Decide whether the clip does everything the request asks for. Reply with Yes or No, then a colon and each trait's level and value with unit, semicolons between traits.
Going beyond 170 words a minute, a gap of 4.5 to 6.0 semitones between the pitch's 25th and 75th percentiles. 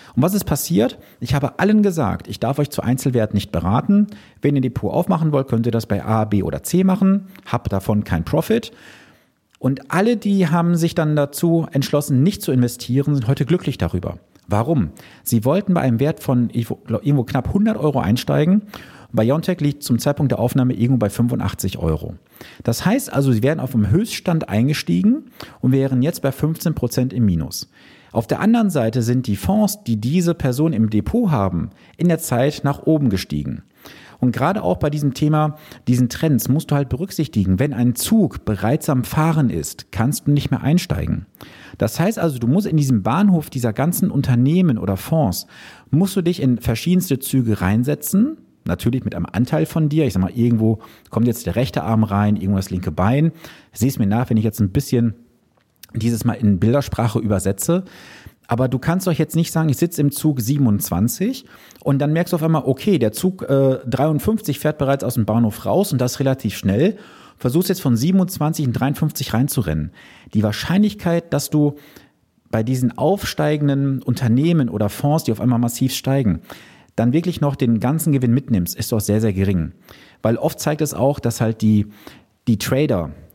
Yes: average, 185 wpm; wide, 5.4 semitones